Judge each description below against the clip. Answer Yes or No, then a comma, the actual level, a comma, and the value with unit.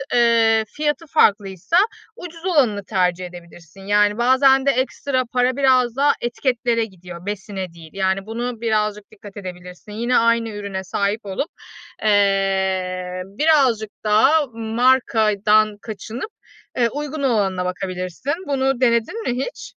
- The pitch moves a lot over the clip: No, average, 4.8 semitones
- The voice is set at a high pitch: Yes, high, 220 Hz